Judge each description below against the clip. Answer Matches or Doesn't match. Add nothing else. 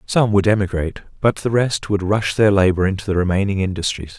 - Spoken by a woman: Doesn't match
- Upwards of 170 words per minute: Matches